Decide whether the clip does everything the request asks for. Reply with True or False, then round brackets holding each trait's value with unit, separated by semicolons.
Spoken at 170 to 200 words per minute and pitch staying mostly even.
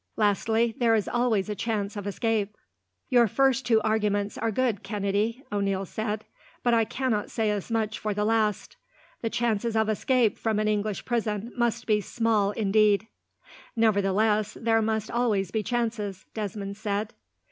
False (160 wpm; 1.8 semitones)